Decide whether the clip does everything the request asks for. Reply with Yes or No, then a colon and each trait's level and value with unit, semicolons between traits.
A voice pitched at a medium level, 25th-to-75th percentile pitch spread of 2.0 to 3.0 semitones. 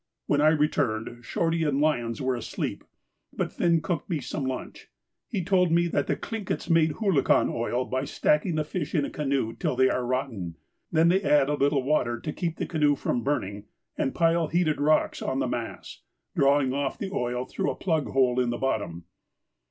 No: medium, 145 Hz; average, 4.3 semitones